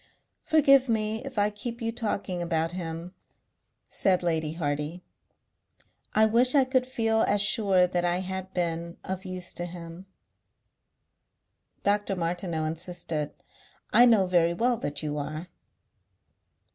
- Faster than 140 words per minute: No, slow, 135 wpm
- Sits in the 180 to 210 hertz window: Yes, medium, 185 Hz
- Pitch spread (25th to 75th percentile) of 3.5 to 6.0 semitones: Yes, average, 4.5 semitones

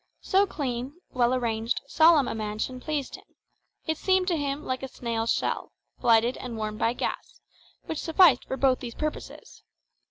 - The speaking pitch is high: Yes, very high, 255 Hz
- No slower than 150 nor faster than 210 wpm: Yes, average, 165 wpm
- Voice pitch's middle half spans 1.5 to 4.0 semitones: No, average, 4.7 semitones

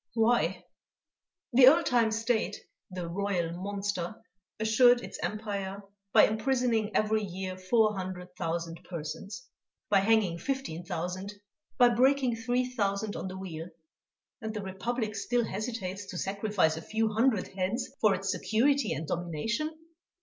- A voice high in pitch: Yes, high, 205 Hz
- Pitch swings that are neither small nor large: Yes, average, 3.9 semitones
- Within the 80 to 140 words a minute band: Yes, slow, 135 wpm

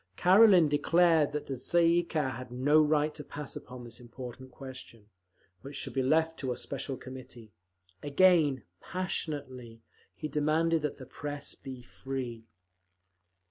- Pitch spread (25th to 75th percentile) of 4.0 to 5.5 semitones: No, average, 3.5 semitones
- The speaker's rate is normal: Yes, average, 145 wpm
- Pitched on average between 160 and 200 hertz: No, medium, 140 Hz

